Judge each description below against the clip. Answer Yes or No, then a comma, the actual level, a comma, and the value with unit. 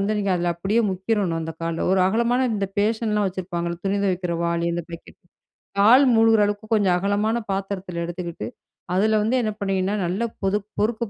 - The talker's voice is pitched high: Yes, high, 195 Hz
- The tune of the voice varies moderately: Yes, average, 3.3 semitones